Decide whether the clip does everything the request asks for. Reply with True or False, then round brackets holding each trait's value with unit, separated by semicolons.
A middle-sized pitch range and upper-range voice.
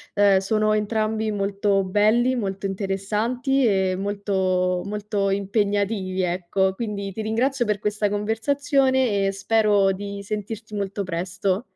False (2.1 semitones; 205 Hz)